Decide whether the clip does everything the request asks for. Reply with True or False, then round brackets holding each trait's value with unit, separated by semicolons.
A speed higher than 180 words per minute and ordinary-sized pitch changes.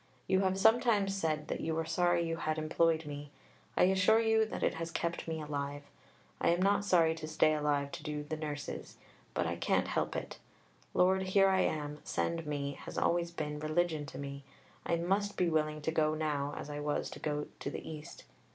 True (205 wpm; 3.3 semitones)